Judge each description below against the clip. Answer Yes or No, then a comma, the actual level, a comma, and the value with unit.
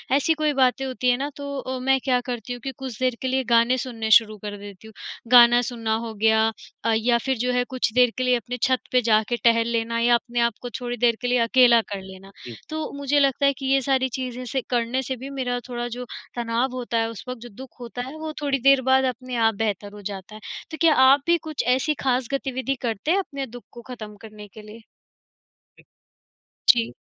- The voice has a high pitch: Yes, high, 245 Hz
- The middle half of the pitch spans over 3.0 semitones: No, narrow, 2.4 semitones